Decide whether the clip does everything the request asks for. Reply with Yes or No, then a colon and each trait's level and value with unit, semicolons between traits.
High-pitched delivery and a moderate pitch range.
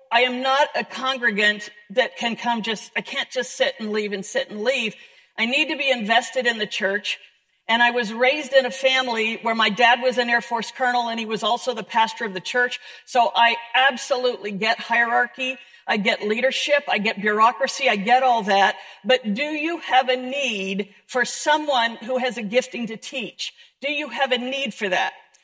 Yes: high, 235 Hz; average, 3.5 semitones